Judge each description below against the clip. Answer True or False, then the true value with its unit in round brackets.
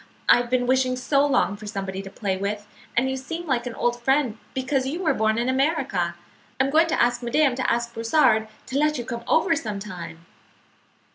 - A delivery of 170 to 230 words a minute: True (205 wpm)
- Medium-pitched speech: False (245 Hz)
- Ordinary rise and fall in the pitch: True (3.9 semitones)